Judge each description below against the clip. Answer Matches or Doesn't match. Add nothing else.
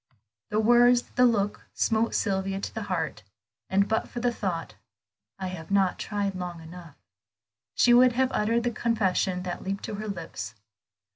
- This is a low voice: Doesn't match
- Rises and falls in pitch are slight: Doesn't match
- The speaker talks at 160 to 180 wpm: Matches